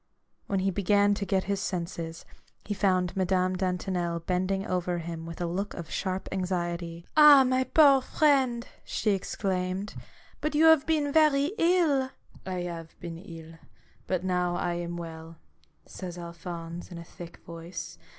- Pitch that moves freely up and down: No, average, 3.3 semitones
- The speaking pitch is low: No, medium, 185 Hz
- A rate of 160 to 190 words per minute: Yes, average, 170 wpm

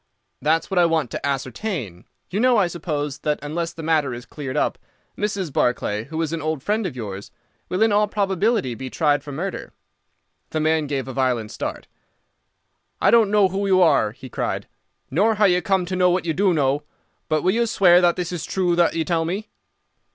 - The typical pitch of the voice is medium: Yes, medium, 165 Hz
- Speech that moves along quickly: Yes, fast, 210 wpm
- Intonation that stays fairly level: No, average, 5.1 semitones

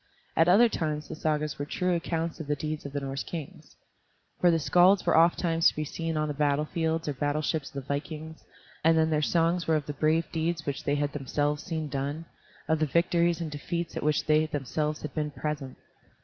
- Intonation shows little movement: Yes, narrow, 2.0 semitones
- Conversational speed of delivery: No, fast, 220 wpm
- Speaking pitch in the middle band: Yes, medium, 155 Hz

